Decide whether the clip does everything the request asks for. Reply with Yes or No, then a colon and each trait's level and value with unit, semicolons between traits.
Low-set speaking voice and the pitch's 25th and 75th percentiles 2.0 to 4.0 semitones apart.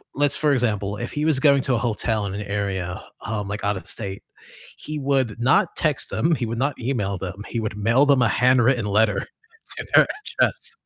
No: low, 115 Hz; average, 4.7 semitones